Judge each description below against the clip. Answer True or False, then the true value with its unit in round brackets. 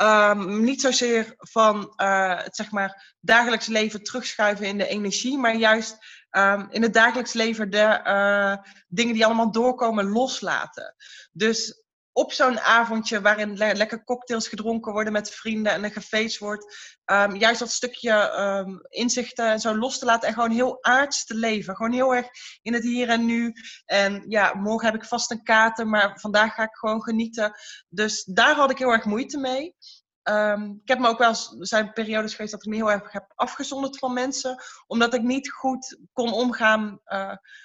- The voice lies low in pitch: False (225 Hz)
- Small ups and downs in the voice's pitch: True (2.3 semitones)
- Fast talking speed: False (175 wpm)